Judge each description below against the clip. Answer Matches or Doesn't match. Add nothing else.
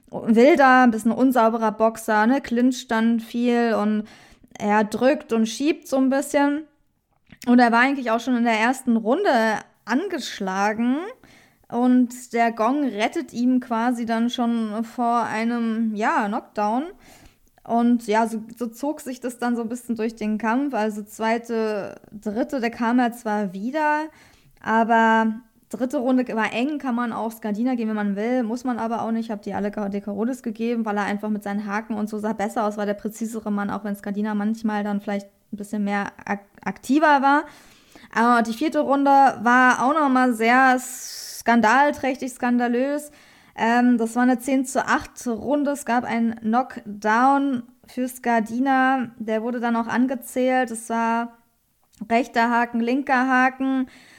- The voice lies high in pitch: Matches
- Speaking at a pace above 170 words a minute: Doesn't match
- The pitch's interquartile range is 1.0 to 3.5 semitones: Matches